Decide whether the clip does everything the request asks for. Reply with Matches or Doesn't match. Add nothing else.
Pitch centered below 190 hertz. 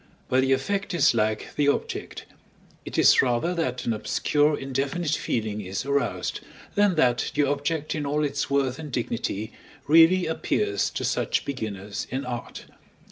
Matches